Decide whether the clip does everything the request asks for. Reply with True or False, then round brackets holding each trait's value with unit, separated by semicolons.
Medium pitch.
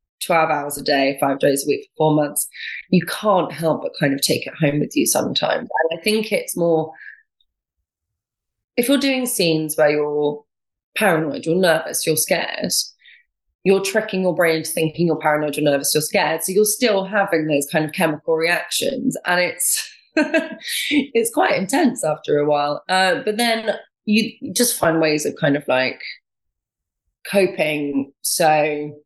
True (160 Hz)